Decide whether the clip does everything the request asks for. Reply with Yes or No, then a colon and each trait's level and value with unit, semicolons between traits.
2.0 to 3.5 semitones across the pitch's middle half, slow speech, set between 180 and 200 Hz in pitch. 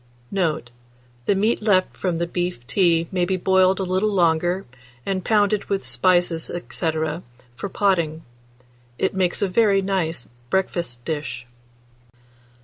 Yes: average, 2.7 semitones; slow, 130 wpm; medium, 185 Hz